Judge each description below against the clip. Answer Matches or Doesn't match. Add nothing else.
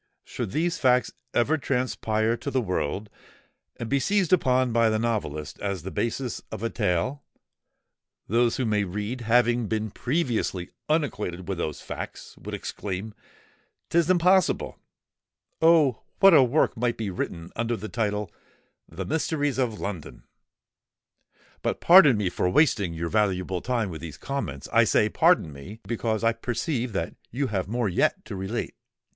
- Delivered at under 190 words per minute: Matches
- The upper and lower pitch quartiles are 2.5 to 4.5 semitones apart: Doesn't match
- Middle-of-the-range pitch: Doesn't match